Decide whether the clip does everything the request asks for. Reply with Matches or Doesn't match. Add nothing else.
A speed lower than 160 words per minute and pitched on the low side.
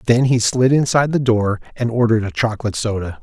Doesn't match